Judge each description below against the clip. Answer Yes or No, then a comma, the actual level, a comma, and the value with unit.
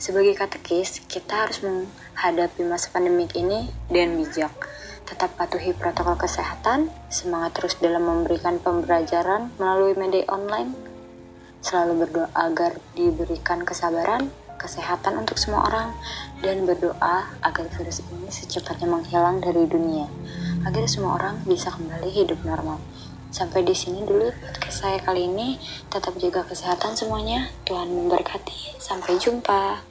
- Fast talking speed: No, average, 125 wpm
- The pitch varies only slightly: Yes, narrow, 2.1 semitones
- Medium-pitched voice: Yes, medium, 175 Hz